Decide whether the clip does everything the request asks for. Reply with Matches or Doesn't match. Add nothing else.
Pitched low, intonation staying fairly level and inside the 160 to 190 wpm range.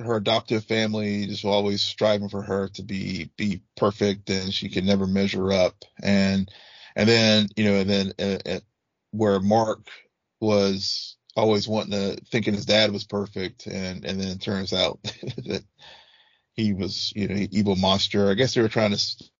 Matches